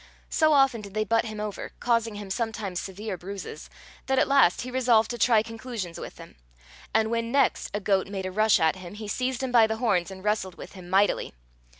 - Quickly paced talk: Yes, fast, 220 wpm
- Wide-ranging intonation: No, average, 3.2 semitones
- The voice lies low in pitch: No, high, 215 Hz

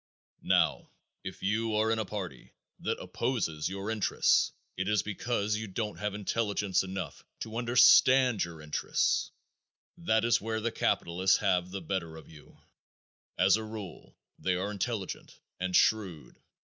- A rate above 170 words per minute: No, average, 145 wpm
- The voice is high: No, low, 105 Hz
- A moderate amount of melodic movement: Yes, average, 3.2 semitones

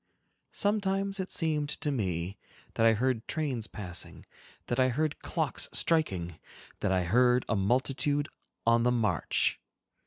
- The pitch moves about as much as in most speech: No, wide, 6.4 semitones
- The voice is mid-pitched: No, low, 125 Hz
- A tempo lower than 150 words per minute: Yes, slow, 135 wpm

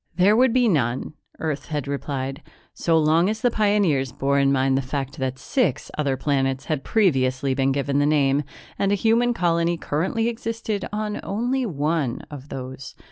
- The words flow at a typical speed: Yes, average, 175 wpm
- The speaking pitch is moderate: Yes, medium, 150 Hz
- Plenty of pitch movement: Yes, wide, 7.2 semitones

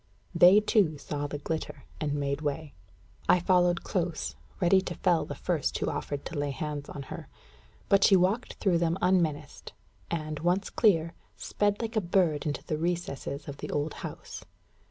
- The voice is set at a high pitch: No, medium, 165 Hz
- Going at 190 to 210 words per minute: No, average, 175 wpm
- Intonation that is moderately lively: Yes, average, 3.8 semitones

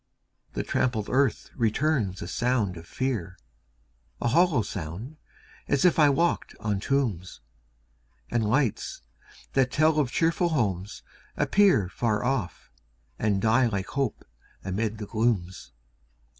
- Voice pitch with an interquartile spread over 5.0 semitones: Yes, wide, 5.5 semitones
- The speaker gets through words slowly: Yes, slow, 125 wpm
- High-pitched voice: No, low, 115 Hz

